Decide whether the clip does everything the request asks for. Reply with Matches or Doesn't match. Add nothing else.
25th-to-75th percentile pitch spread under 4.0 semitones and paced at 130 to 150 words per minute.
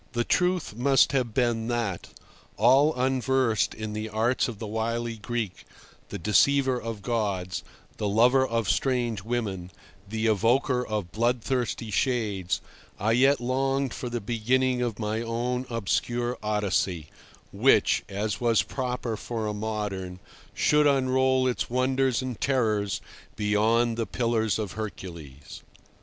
Matches